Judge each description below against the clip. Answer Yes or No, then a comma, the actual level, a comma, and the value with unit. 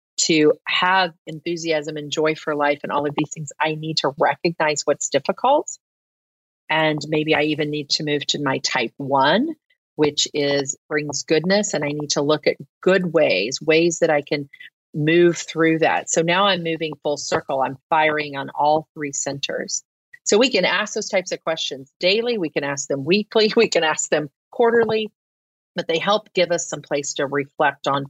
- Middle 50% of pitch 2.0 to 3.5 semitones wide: Yes, average, 3.1 semitones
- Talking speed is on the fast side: No, average, 190 wpm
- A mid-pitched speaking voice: Yes, medium, 155 Hz